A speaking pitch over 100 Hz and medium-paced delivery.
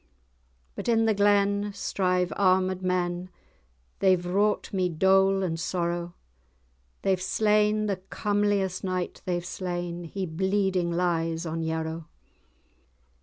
No: medium, 185 Hz; slow, 110 wpm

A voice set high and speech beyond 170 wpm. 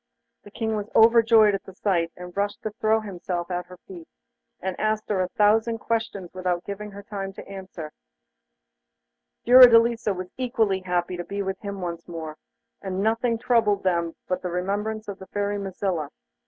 Yes: high, 200 Hz; average, 180 wpm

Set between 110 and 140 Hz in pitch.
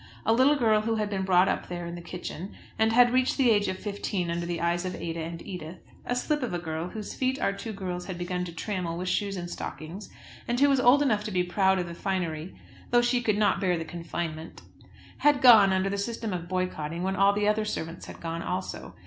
No: high, 190 Hz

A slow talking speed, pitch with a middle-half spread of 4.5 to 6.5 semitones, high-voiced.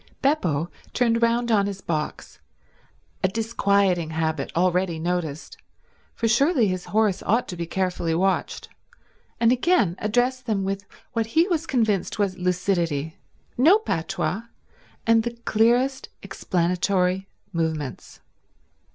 Yes: slow, 110 wpm; average, 4.8 semitones; high, 195 Hz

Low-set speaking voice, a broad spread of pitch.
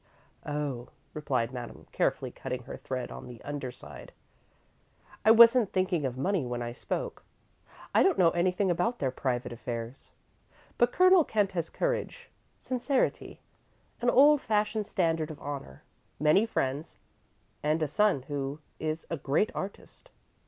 No: medium, 160 Hz; wide, 8.0 semitones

